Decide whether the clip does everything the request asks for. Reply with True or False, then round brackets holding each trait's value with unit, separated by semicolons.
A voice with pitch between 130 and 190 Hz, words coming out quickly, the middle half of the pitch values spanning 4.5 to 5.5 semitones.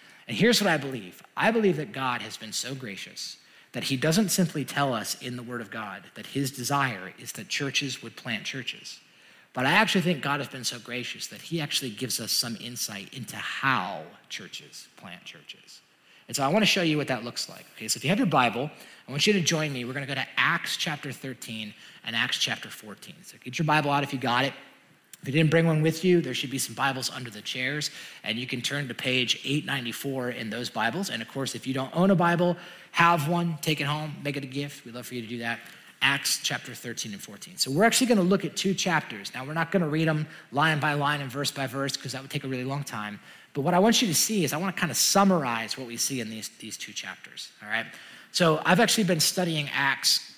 True (140 Hz; 255 wpm; 4.8 semitones)